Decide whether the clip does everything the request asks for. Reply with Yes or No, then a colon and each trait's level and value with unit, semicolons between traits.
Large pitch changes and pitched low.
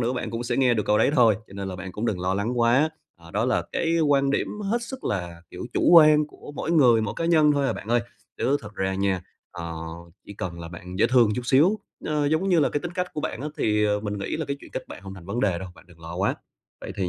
Yes: wide, 7.5 semitones; low, 115 Hz